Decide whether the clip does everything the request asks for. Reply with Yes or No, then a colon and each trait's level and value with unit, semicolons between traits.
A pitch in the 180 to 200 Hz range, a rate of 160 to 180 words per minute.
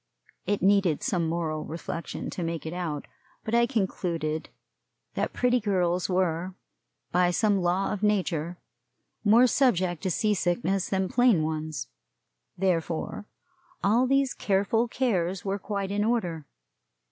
No: medium, 185 Hz; slow, 135 wpm